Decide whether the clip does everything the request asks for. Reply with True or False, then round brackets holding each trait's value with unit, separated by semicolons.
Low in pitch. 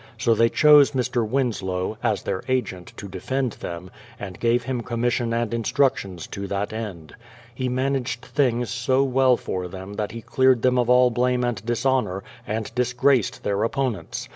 True (120 Hz)